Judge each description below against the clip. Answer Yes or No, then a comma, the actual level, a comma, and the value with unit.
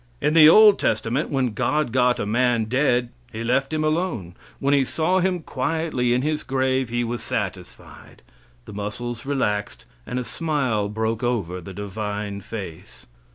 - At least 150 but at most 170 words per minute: Yes, average, 160 wpm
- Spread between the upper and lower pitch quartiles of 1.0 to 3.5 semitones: No, average, 5.1 semitones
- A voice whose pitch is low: Yes, low, 125 Hz